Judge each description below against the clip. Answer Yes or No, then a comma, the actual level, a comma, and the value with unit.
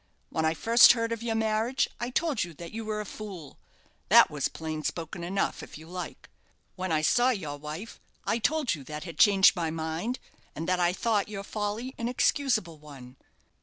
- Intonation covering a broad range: Yes, wide, 6.2 semitones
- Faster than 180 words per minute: Yes, average, 200 wpm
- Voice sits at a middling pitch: No, high, 195 Hz